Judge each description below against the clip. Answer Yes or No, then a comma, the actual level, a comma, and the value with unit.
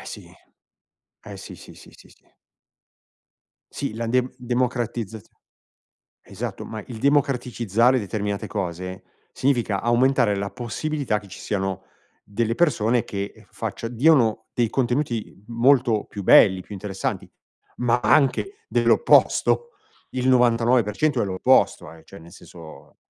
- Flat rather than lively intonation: No, average, 3.7 semitones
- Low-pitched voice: Yes, low, 115 Hz